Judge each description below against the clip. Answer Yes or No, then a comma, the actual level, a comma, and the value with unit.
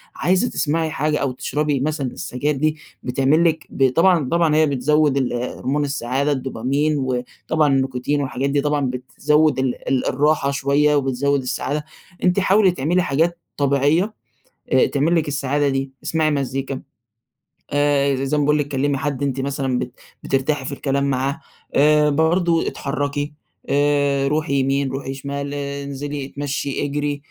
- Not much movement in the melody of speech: Yes, narrow, 1.8 semitones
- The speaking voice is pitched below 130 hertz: No, medium, 140 Hz